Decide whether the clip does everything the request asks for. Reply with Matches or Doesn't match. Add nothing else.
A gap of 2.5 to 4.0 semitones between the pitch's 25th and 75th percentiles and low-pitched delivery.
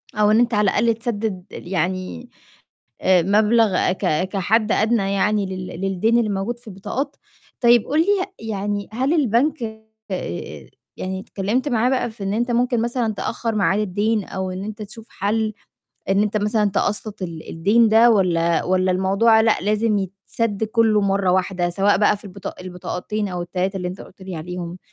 Doesn't match